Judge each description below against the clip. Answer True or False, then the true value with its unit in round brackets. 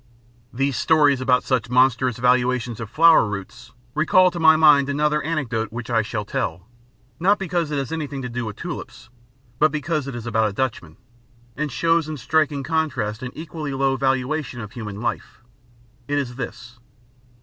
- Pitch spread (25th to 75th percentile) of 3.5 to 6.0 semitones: True (4.4 semitones)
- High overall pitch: False (130 Hz)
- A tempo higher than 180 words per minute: False (170 wpm)